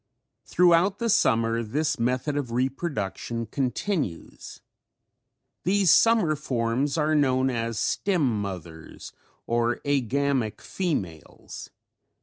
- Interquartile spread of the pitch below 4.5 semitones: No, average, 5.2 semitones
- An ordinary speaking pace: No, slow, 100 wpm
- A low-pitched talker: Yes, low, 130 Hz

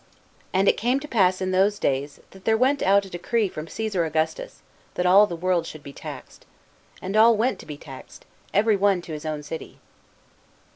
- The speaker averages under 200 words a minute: No, fast, 205 wpm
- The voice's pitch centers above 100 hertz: Yes, medium, 185 Hz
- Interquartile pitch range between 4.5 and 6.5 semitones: Yes, average, 5.0 semitones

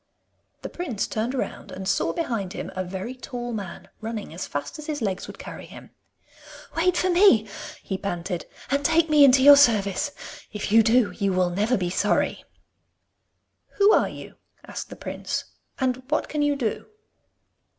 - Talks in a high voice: Yes, high, 230 Hz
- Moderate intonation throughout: No, wide, 6.7 semitones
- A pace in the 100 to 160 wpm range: No, average, 170 wpm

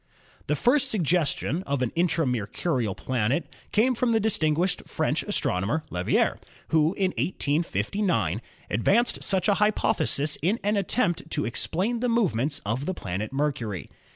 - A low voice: No, medium, 160 Hz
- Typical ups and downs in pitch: No, wide, 8.1 semitones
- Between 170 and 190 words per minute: No, average, 140 wpm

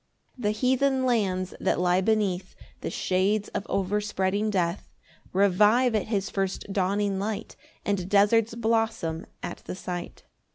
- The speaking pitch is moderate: No, high, 200 Hz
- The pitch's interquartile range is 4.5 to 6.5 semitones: No, average, 2.8 semitones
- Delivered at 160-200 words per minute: No, slow, 135 wpm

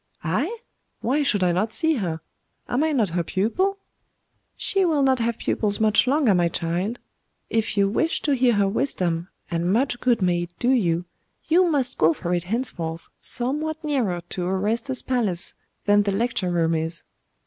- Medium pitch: No, high, 215 Hz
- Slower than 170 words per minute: No, average, 175 wpm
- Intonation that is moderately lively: No, wide, 6.9 semitones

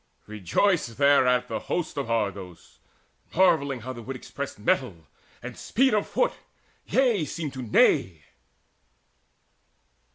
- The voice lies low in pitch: Yes, low, 130 Hz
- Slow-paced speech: Yes, slow, 120 wpm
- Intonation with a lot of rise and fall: Yes, wide, 7.8 semitones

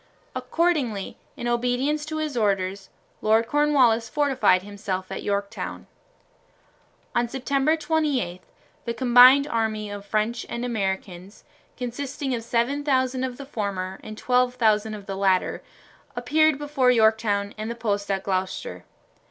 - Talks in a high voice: Yes, high, 235 Hz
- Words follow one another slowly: Yes, slow, 125 wpm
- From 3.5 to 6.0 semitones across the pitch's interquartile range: Yes, average, 4.8 semitones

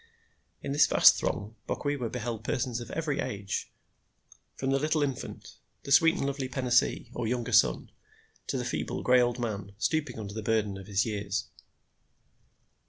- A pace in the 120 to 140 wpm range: No, average, 165 wpm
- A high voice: No, low, 120 Hz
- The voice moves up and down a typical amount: Yes, average, 4.3 semitones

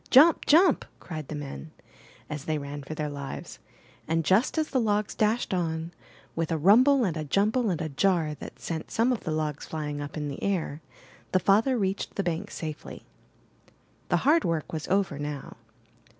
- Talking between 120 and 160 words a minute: No, average, 185 wpm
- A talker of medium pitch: Yes, medium, 165 Hz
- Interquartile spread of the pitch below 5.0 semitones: No, wide, 5.6 semitones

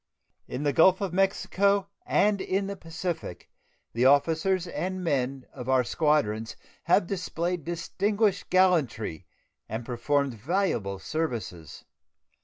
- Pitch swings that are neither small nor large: No, wide, 6.8 semitones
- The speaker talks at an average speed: No, slow, 115 wpm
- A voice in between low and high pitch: Yes, medium, 165 Hz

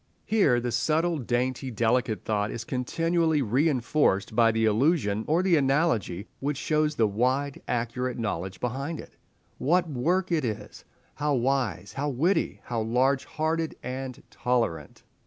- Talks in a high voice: No, low, 130 Hz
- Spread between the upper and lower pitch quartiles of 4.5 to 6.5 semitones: Yes, average, 5.0 semitones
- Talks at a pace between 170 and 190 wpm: No, average, 140 wpm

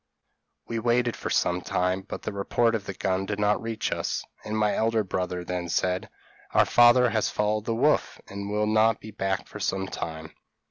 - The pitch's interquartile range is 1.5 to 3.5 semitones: Yes, average, 3.0 semitones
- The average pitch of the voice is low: Yes, low, 105 Hz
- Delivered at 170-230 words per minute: Yes, average, 200 wpm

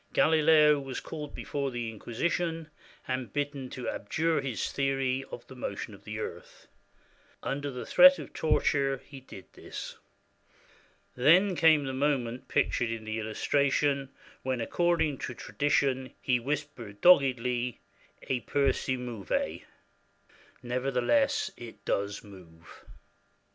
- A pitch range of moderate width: Yes, average, 3.4 semitones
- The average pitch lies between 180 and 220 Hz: No, low, 135 Hz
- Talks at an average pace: No, slow, 125 wpm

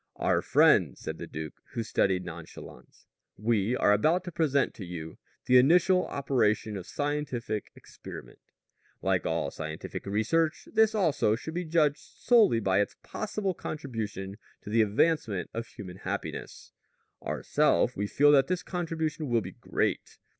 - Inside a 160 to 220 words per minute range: No, average, 145 wpm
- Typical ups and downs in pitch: No, wide, 7.9 semitones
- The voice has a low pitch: Yes, low, 125 Hz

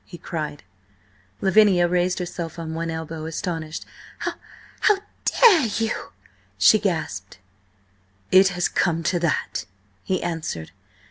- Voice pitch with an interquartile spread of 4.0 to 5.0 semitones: No, average, 2.8 semitones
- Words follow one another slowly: Yes, slow, 120 wpm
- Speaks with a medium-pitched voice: Yes, medium, 170 Hz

